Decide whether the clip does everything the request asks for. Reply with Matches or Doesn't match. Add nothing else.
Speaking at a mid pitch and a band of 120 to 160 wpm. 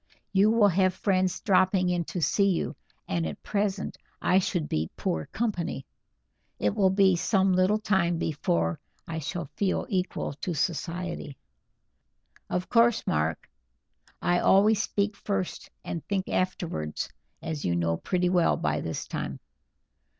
Matches